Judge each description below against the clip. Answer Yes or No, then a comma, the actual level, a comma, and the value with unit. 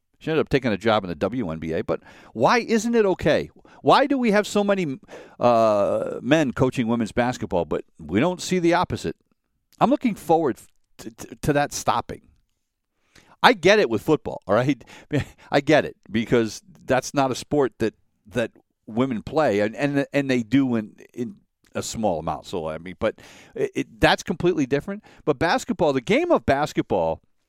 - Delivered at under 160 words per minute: No, average, 180 wpm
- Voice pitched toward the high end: No, medium, 140 Hz